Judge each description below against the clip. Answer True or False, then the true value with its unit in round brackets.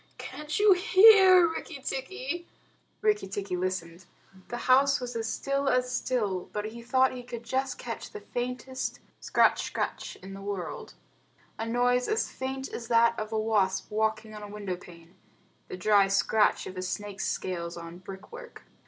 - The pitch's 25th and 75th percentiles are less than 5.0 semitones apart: False (5.4 semitones)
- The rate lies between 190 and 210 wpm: False (170 wpm)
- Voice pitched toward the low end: False (230 Hz)